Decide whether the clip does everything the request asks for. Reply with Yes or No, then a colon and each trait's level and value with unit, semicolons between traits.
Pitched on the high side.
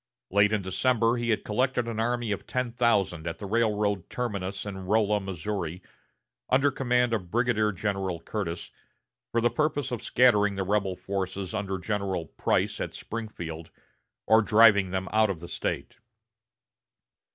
No: low, 105 Hz